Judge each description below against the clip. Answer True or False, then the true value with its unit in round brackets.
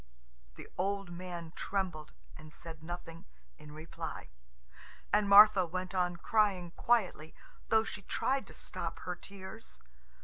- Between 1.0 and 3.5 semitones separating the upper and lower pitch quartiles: True (3.1 semitones)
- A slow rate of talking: True (130 wpm)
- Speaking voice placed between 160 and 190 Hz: True (185 Hz)